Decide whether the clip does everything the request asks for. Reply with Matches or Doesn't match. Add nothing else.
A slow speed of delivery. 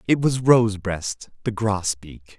Matches